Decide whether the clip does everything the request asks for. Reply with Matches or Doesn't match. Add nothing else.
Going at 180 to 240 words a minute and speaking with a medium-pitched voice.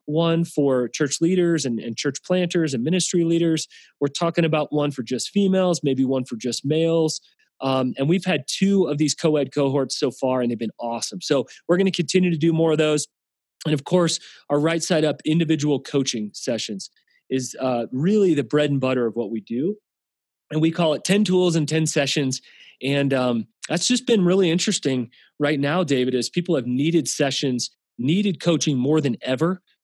Matches